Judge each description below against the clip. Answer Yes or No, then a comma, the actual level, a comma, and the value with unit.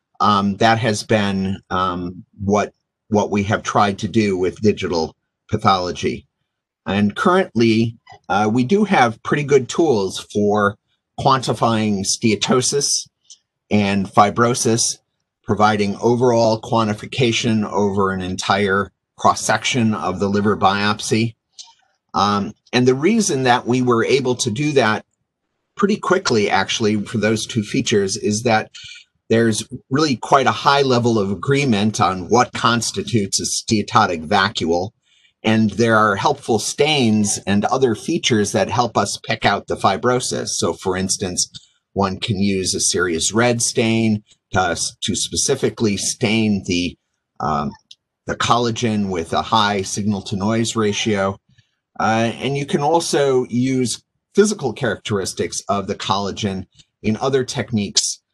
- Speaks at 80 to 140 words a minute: Yes, slow, 135 wpm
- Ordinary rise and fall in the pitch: Yes, average, 3.2 semitones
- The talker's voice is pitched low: Yes, low, 110 Hz